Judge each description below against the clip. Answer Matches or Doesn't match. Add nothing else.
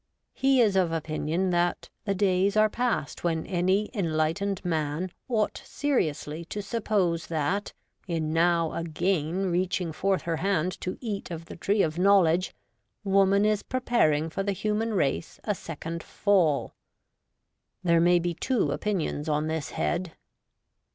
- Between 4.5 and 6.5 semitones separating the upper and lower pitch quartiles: Doesn't match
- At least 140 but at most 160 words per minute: Matches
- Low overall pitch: Doesn't match